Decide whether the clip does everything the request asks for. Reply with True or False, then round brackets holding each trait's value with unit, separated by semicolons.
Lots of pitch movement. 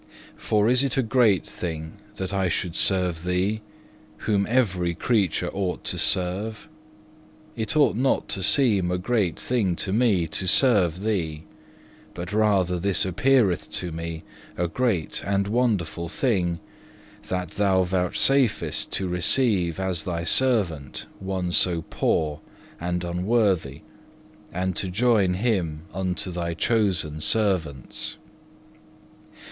False (3.8 semitones)